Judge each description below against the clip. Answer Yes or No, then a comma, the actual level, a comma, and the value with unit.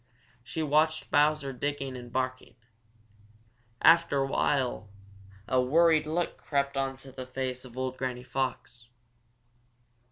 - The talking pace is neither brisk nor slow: No, slow, 120 wpm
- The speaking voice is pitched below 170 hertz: Yes, low, 135 Hz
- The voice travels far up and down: No, average, 2.7 semitones